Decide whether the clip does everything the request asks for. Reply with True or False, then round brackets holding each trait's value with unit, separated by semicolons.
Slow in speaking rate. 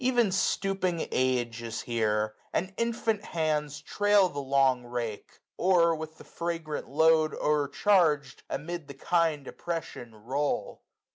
True (125 wpm)